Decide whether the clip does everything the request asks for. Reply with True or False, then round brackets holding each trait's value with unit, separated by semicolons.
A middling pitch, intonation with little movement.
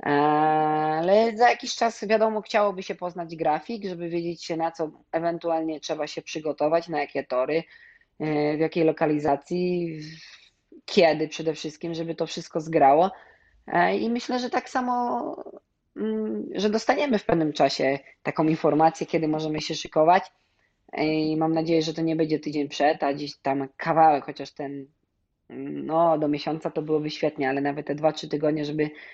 True (160 Hz; 2.2 semitones)